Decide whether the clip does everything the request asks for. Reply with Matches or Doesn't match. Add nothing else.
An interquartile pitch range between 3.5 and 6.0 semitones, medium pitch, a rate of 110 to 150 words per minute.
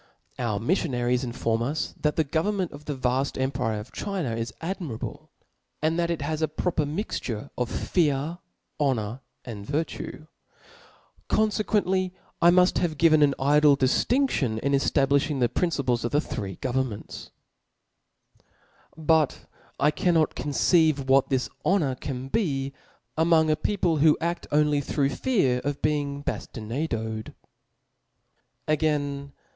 Matches